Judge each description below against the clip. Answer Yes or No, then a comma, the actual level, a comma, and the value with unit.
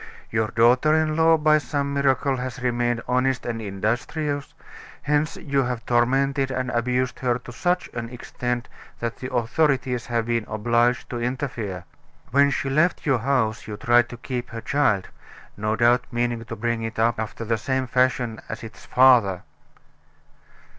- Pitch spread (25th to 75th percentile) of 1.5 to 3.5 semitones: Yes, narrow, 2.5 semitones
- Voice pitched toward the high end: No, low, 125 Hz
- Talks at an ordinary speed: Yes, average, 160 wpm